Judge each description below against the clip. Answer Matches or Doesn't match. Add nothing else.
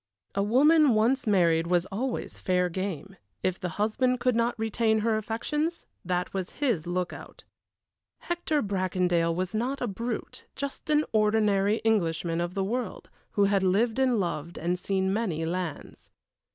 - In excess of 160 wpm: Doesn't match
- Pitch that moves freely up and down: Doesn't match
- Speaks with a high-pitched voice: Matches